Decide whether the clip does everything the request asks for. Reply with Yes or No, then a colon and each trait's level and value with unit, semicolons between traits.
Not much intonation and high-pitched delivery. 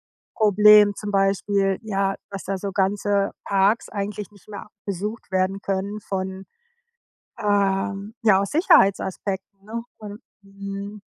Yes: narrow, 1.2 semitones; high, 200 Hz